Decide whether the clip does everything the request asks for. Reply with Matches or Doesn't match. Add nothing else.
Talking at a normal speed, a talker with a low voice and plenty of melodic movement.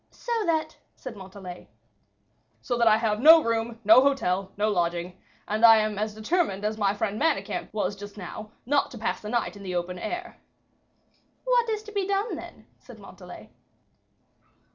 Doesn't match